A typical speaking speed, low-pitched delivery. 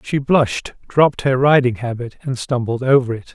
Yes: average, 180 wpm; low, 130 Hz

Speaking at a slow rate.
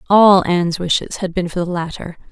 No: fast, 205 wpm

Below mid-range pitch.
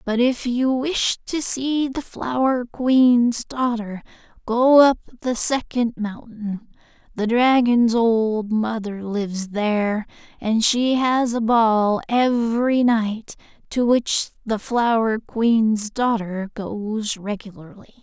No: high, 230 Hz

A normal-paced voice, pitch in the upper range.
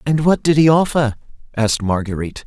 No: average, 170 wpm; low, 130 Hz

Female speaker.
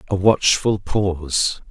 No: male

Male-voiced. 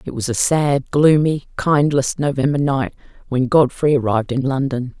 No: female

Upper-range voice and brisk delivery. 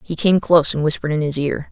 No: medium, 155 Hz; fast, 280 wpm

